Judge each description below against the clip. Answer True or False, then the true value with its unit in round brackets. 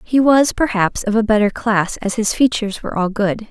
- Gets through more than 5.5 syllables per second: False (5.3 syllables/s)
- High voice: True (215 Hz)